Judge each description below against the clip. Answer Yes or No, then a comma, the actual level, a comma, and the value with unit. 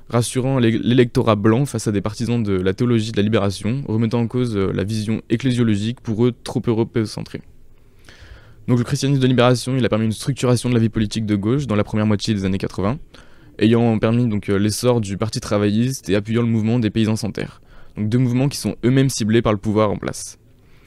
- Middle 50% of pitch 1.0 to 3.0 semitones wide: Yes, narrow, 2.4 semitones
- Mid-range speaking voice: No, low, 115 Hz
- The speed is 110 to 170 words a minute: No, average, 215 wpm